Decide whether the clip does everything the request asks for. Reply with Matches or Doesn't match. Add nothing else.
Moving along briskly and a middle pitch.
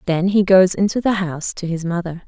Matches